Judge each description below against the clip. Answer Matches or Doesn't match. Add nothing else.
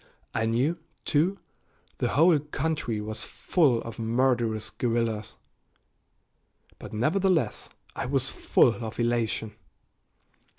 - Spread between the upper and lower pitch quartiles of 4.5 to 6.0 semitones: Matches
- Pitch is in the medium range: Doesn't match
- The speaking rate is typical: Doesn't match